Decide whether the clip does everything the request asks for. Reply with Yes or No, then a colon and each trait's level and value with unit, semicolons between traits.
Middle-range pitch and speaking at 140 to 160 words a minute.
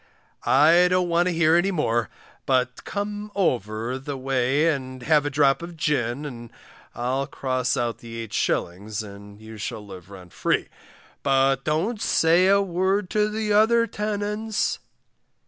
Yes: medium, 145 Hz; average, 150 wpm